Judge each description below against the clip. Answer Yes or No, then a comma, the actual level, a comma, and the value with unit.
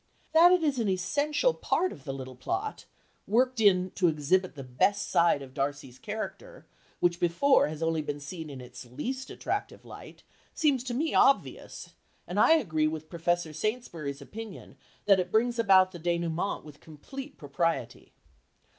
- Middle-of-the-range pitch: Yes, medium, 180 Hz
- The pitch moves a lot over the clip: Yes, wide, 8.1 semitones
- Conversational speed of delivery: Yes, average, 165 wpm